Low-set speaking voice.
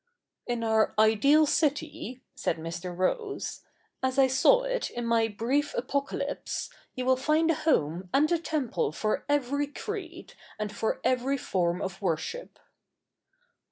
No: very high, 260 Hz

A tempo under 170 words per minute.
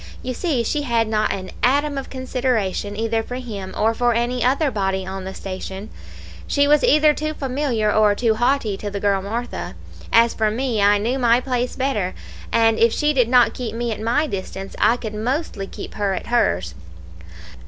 No: average, 195 wpm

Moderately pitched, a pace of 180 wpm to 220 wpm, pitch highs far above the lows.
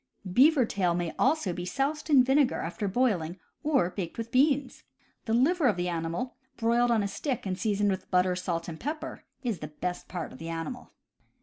No: high, 210 Hz; average, 200 wpm; wide, 6.8 semitones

